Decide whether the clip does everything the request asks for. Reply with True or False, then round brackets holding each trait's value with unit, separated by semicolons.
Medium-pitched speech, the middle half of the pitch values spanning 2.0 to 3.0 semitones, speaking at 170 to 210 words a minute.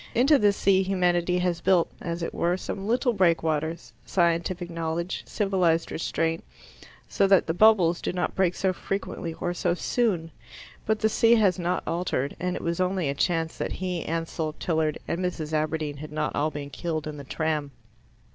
True (170 Hz; 2.6 semitones; 180 wpm)